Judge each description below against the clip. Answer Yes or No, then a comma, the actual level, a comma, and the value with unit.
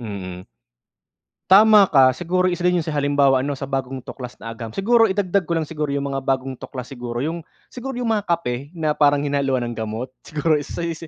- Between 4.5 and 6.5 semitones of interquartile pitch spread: Yes, average, 4.9 semitones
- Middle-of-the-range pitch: Yes, medium, 145 Hz